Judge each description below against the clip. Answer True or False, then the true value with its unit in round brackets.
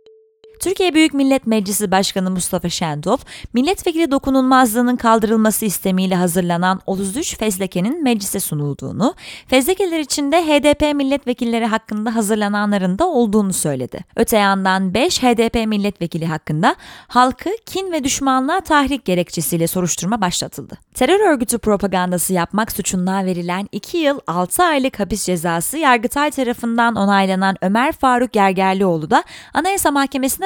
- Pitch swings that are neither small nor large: False (6.5 semitones)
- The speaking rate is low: False (120 wpm)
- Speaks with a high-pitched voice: True (225 Hz)